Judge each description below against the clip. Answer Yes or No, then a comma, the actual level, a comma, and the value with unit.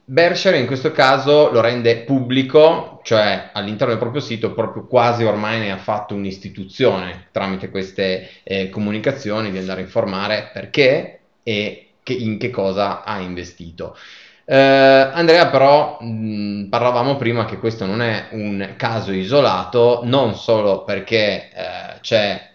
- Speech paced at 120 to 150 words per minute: Yes, average, 140 wpm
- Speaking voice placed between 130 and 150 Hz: No, low, 115 Hz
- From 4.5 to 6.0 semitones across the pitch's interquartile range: Yes, wide, 5.4 semitones